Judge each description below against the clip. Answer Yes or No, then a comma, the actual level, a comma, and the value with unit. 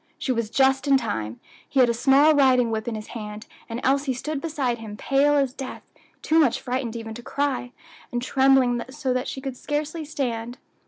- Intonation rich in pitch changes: No, average, 3.0 semitones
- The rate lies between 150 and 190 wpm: No, average, 200 wpm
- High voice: Yes, very high, 260 Hz